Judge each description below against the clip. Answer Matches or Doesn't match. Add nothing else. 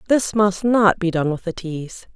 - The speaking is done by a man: Doesn't match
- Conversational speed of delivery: Doesn't match